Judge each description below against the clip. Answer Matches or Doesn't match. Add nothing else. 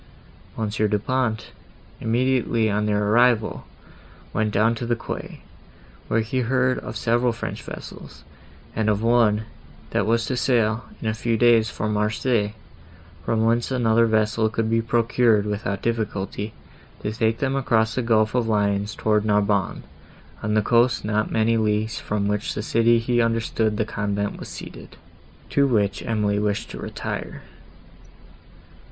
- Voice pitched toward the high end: Doesn't match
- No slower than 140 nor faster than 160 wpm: Matches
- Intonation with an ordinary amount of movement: Doesn't match